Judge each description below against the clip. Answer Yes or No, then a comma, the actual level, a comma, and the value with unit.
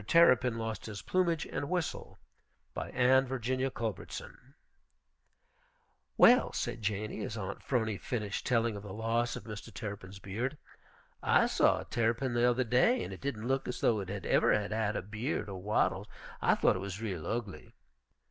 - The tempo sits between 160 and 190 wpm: Yes, average, 170 wpm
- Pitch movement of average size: Yes, average, 3.5 semitones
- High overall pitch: No, low, 115 Hz